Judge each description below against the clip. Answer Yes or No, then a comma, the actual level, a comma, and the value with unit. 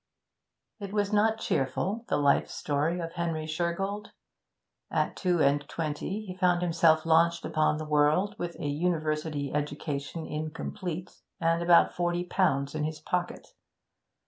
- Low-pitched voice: No, medium, 165 Hz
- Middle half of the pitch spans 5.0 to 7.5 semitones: No, average, 2.8 semitones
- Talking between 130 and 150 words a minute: Yes, average, 140 wpm